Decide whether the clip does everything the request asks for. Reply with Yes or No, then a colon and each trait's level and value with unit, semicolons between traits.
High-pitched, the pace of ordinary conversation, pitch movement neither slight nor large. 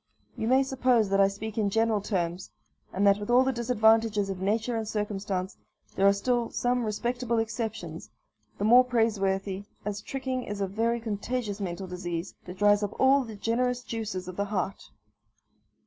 Yes: high, 215 Hz; average, 175 wpm; average, 3.2 semitones